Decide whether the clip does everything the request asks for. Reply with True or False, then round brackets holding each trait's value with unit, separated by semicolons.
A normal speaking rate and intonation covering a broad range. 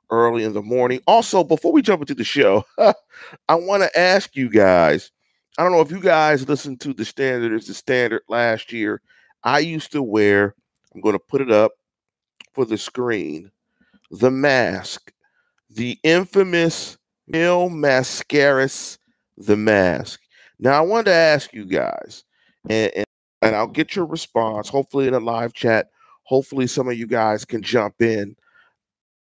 True (165 wpm; 6.2 semitones)